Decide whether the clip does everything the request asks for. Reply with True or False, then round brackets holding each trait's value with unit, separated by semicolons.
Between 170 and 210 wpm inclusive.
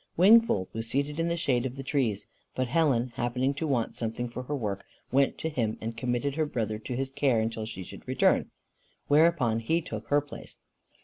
True (200 wpm)